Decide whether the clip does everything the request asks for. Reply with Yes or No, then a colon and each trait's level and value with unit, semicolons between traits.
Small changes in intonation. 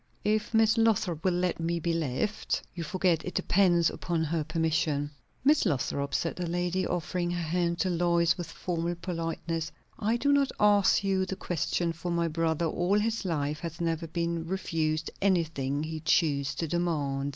Yes: narrow, 2.3 semitones